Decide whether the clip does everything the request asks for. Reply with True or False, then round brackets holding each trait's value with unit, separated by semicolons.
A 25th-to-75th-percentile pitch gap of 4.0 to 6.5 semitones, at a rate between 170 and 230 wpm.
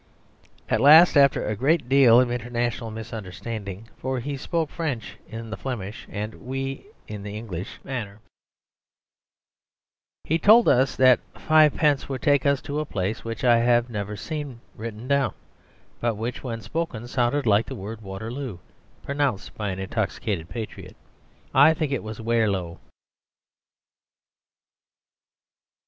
False (4.3 semitones; 135 wpm)